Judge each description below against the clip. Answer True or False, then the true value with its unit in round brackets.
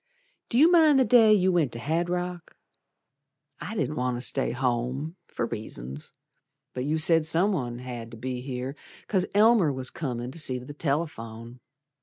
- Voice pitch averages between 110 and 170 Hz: True (140 Hz)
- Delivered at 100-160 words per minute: False (175 wpm)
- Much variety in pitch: True (6.2 semitones)